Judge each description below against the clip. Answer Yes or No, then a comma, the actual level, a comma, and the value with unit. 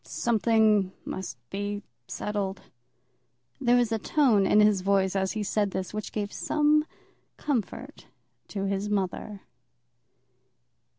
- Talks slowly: Yes, slow, 120 wpm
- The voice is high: Yes, high, 205 Hz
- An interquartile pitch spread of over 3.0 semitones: No, narrow, 2.4 semitones